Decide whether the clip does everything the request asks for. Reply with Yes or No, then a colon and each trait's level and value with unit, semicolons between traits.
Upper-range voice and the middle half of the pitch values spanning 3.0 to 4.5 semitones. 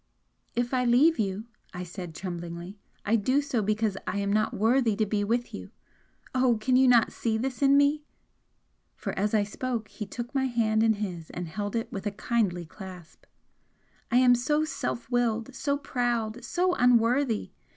Yes: high, 225 Hz; average, 3.7 semitones